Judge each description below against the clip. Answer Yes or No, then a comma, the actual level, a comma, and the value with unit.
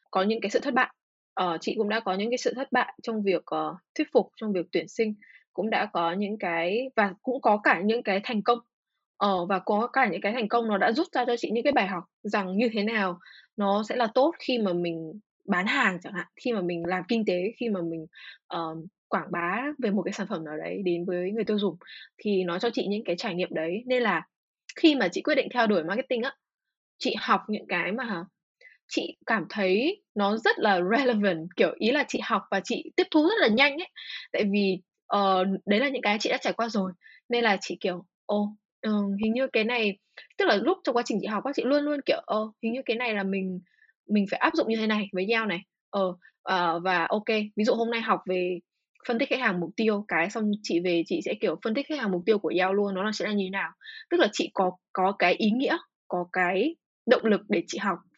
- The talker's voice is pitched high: Yes, high, 210 Hz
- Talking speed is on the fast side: Yes, fast, 255 wpm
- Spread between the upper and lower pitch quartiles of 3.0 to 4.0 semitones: No, average, 4.4 semitones